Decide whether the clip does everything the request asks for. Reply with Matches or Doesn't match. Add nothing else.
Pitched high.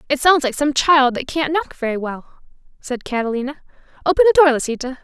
Matches